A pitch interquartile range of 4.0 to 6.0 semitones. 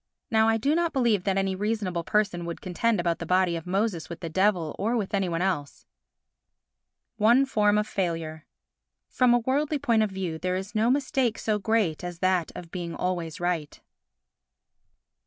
Yes: average, 4.4 semitones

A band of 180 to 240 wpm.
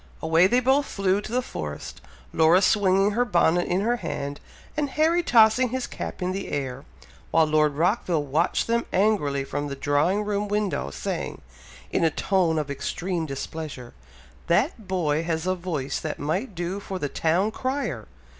No: average, 170 wpm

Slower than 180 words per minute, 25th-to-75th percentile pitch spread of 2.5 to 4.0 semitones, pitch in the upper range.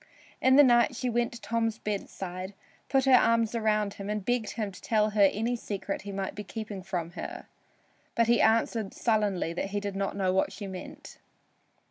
No: average, 195 wpm; average, 2.9 semitones; high, 210 Hz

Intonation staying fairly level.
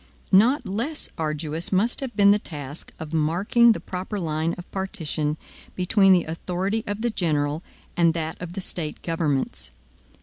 No: average, 4.3 semitones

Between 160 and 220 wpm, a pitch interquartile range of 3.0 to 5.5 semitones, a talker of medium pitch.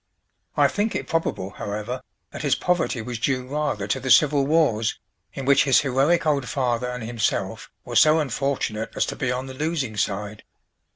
No: average, 180 wpm; average, 4.2 semitones; low, 130 Hz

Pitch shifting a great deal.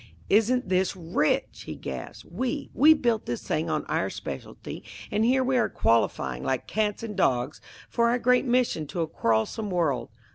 Yes: wide, 8.2 semitones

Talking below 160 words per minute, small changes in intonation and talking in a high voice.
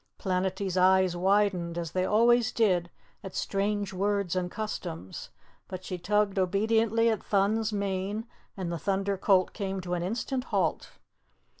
Yes: average, 145 wpm; narrow, 2.3 semitones; high, 195 Hz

